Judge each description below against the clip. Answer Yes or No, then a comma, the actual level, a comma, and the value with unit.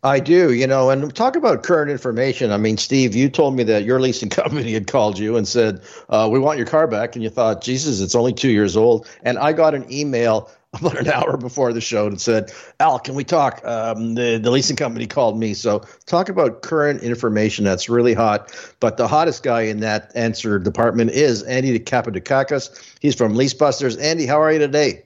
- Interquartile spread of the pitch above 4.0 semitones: No, average, 3.5 semitones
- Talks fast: Yes, fast, 215 wpm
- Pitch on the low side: Yes, low, 120 Hz